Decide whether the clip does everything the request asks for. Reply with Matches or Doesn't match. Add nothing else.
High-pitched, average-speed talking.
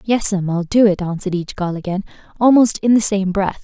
Doesn't match